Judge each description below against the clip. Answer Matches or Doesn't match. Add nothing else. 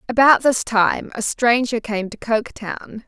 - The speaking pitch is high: Matches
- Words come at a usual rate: Matches